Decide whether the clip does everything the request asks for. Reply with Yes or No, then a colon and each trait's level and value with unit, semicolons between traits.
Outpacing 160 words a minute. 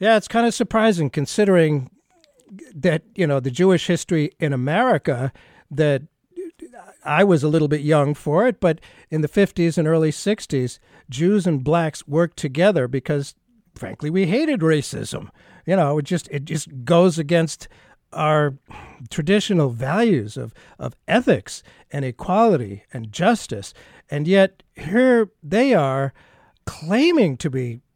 No: average, 140 wpm